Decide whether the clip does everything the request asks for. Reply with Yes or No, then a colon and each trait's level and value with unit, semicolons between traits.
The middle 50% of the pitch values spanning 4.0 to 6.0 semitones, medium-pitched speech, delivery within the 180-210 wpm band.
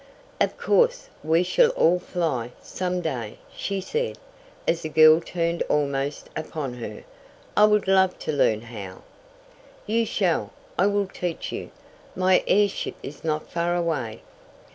No: average, 4.8 semitones; medium, 170 Hz; average, 140 wpm